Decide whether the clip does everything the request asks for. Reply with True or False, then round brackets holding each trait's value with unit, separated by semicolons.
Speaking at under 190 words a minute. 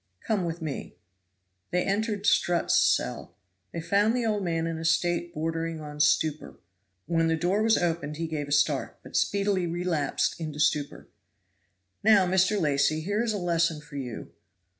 True (165 wpm)